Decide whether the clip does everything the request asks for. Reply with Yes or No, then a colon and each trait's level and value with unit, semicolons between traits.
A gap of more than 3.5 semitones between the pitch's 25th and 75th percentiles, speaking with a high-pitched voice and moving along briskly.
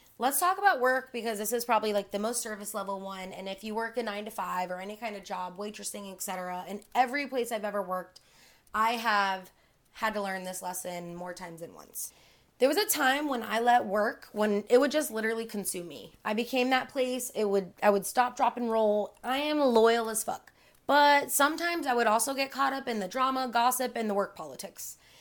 Yes: average, 4.1 semitones; high, 220 Hz; fast, 225 wpm